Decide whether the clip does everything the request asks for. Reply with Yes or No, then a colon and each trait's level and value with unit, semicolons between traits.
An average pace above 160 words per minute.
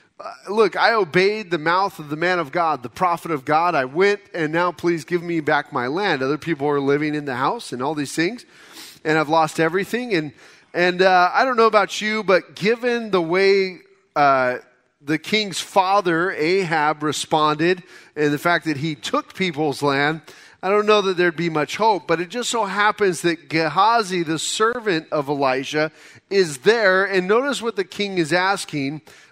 Yes: fast, 205 wpm